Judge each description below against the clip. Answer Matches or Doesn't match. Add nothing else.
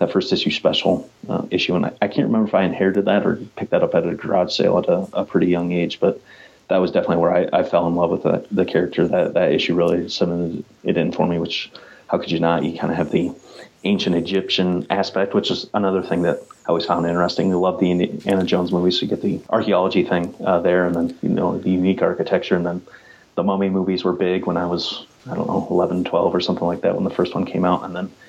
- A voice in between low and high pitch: Doesn't match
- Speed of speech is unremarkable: Doesn't match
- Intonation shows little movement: Matches